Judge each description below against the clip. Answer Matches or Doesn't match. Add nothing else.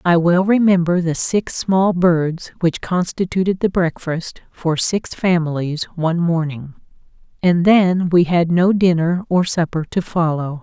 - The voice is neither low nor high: Matches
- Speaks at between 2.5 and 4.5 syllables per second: Matches